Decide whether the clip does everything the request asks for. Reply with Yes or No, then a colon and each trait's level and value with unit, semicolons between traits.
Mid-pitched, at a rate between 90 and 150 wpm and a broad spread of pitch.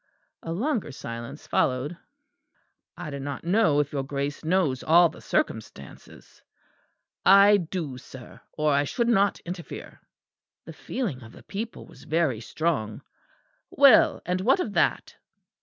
Yes: medium, 160 Hz; average, 140 wpm; wide, 6.1 semitones